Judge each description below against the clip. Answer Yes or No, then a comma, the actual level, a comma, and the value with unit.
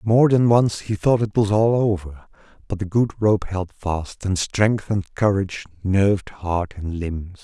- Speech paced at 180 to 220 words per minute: Yes, average, 185 wpm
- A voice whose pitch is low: Yes, low, 100 Hz